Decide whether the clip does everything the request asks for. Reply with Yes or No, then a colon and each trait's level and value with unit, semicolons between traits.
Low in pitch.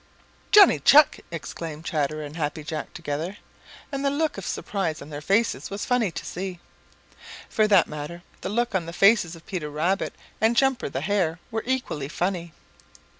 No: medium, 180 Hz